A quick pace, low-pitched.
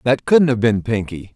Yes: fast, 220 wpm; low, 120 Hz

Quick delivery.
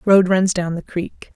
Yes: fast, 220 wpm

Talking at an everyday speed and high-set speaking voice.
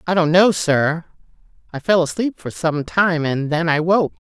No: average, 195 wpm; medium, 165 Hz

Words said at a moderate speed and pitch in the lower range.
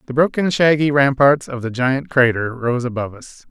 Yes: average, 190 wpm; low, 130 Hz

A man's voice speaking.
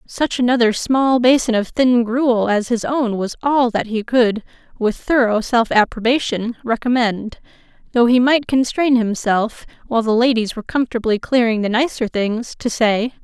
No: female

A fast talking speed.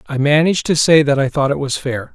Yes: fast, 280 wpm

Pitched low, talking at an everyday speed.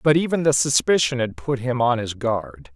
No: low, 125 Hz; fast, 220 wpm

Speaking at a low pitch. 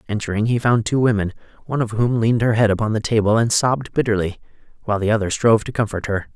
Yes: low, 110 Hz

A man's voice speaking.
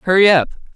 Yes: male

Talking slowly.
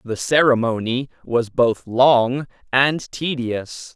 Yes: slow, 105 wpm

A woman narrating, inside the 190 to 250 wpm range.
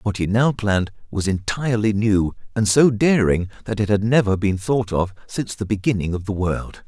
No: male; average, 200 wpm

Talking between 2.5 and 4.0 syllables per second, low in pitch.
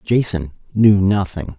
Yes: 3.9 syllables/s; very low, 95 Hz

